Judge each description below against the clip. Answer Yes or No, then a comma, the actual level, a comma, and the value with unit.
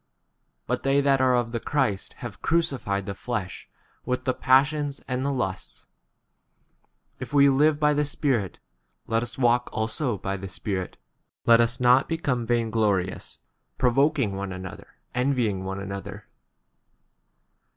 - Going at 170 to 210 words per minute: No, average, 150 wpm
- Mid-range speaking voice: No, low, 120 Hz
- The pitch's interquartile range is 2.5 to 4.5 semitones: No, wide, 5.6 semitones